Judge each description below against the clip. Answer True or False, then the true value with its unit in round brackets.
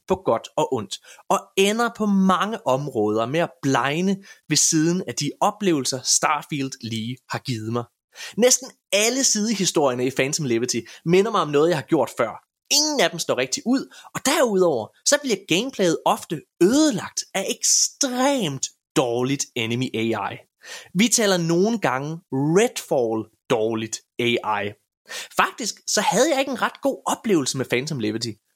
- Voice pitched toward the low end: False (165 Hz)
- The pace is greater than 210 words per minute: False (155 wpm)